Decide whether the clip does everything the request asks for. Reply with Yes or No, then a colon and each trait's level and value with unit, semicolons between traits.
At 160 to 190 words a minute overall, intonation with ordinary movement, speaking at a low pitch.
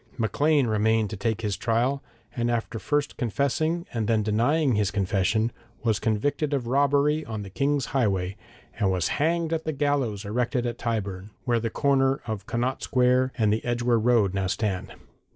Yes: average, 170 wpm; average, 4.6 semitones; low, 120 Hz